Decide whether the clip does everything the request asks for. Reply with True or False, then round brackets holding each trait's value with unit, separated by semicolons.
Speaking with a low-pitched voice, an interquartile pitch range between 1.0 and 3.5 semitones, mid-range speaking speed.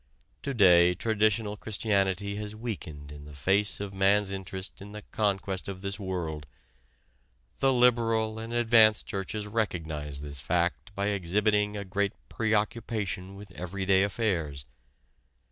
False (100 Hz; 2.8 semitones; 130 wpm)